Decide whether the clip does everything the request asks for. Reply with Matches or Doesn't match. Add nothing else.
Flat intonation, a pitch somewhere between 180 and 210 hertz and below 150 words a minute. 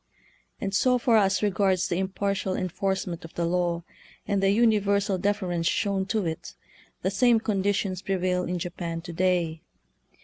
Doesn't match